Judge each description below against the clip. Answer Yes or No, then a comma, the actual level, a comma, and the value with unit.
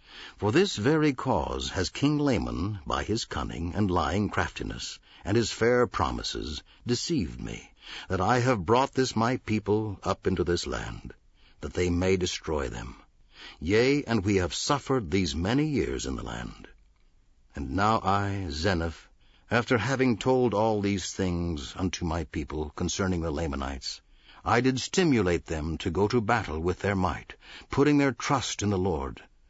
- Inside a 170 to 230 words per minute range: No, average, 160 wpm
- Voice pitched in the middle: No, very low, 95 Hz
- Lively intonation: Yes, wide, 5.7 semitones